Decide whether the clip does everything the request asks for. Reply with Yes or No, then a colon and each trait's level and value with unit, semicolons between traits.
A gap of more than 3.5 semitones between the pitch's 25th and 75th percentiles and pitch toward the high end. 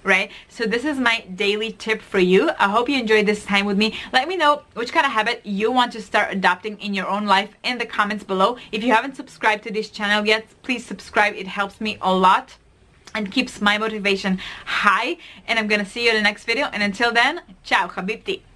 No: narrow, 2.5 semitones; high, 215 Hz